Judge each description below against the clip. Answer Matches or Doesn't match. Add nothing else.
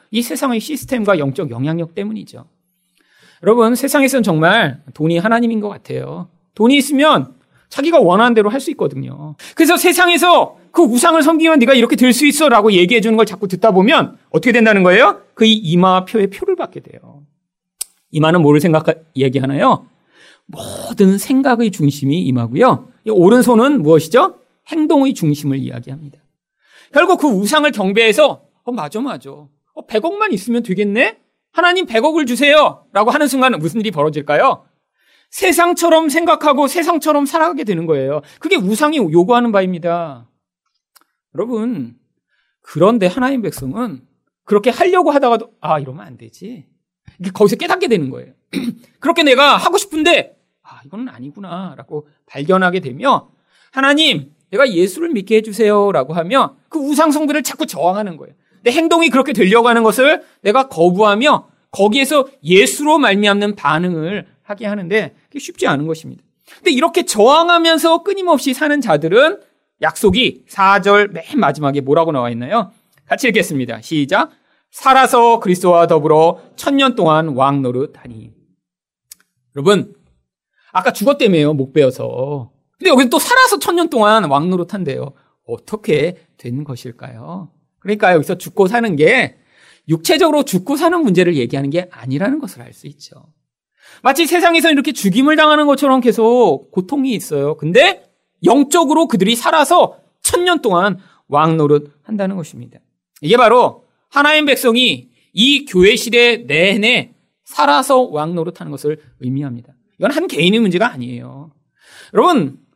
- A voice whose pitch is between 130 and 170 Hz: Doesn't match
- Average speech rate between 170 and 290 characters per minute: Doesn't match